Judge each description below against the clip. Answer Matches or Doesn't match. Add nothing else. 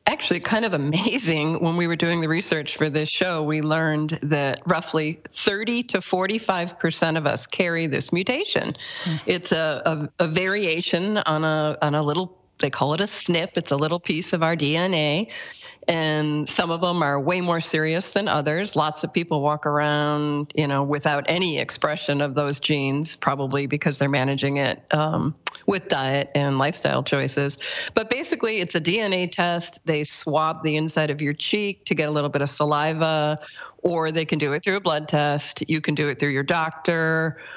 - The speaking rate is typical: Matches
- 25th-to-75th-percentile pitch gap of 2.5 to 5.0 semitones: Matches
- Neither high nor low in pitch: Matches